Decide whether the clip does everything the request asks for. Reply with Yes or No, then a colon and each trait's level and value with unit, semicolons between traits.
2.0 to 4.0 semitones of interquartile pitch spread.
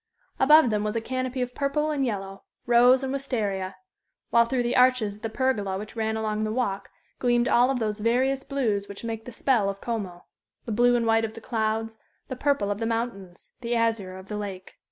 Yes: average, 3.1 semitones